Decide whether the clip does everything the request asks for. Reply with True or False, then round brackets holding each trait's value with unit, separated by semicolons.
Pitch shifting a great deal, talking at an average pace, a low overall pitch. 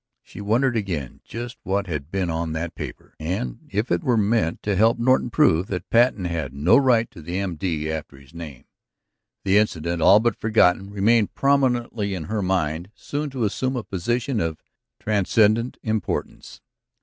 True (5.7 semitones; 170 wpm; 100 Hz)